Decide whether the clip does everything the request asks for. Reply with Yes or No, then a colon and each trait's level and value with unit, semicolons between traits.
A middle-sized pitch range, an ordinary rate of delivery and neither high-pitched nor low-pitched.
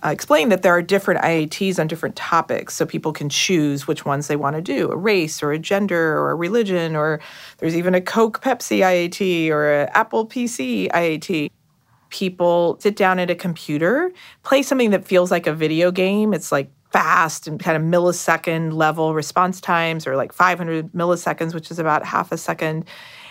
Yes: average, 3.1 semitones; average, 190 wpm; medium, 170 Hz